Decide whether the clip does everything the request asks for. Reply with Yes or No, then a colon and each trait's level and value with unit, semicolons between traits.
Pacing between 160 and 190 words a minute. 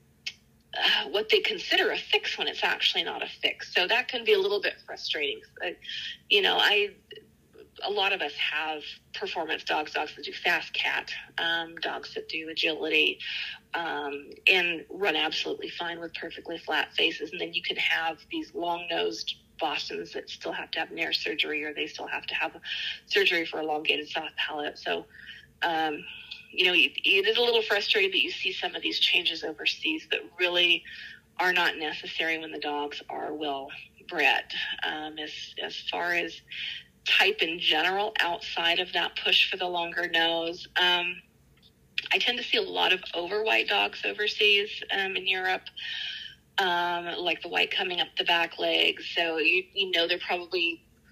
Yes: average, 180 wpm